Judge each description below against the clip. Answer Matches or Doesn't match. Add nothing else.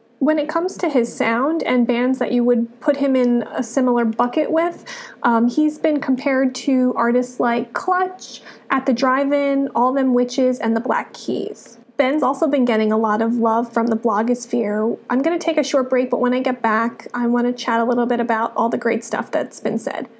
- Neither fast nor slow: Doesn't match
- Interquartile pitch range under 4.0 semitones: Matches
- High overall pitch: Matches